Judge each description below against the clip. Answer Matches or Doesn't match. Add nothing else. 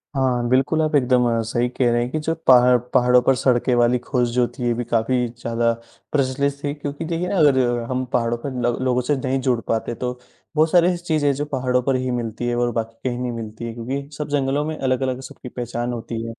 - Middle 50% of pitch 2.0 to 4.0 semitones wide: Matches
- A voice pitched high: Doesn't match